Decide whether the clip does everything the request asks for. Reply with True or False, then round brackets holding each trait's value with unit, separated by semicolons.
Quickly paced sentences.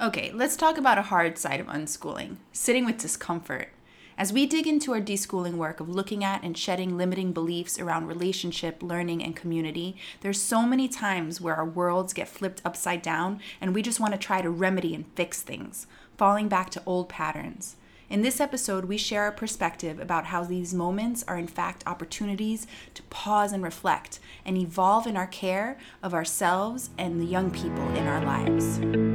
False (185 wpm)